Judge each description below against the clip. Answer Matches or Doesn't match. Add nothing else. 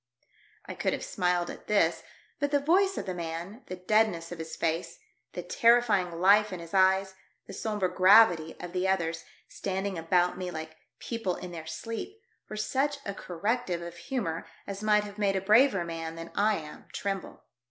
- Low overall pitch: Doesn't match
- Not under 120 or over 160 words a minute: Doesn't match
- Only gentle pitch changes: Doesn't match